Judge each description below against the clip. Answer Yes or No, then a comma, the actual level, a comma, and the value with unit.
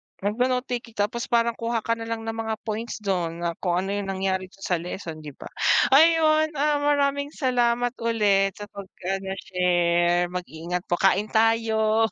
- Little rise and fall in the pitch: No, average, 4.3 semitones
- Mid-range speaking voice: No, high, 215 Hz